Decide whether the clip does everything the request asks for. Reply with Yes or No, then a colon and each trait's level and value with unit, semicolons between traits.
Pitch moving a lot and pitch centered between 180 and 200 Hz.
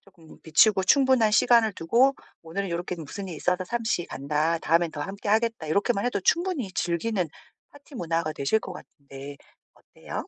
Yes: wide, 5.7 semitones; high, 190 Hz